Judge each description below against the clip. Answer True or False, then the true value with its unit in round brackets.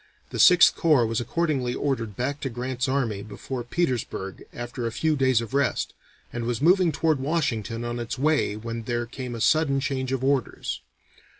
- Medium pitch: False (130 Hz)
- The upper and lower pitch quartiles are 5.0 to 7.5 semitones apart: False (3.3 semitones)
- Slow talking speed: False (180 wpm)